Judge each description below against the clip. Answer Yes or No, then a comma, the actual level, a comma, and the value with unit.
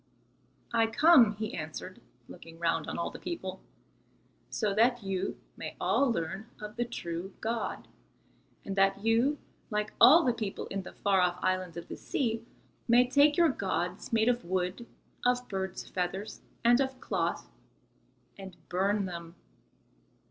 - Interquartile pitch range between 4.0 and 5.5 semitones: Yes, average, 4.4 semitones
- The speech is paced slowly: No, average, 150 wpm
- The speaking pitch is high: Yes, high, 210 Hz